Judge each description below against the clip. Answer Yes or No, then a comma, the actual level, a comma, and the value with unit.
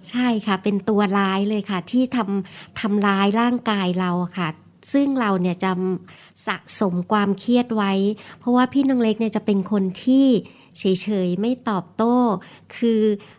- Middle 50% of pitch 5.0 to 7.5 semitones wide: No, average, 3.7 semitones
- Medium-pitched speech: No, high, 205 Hz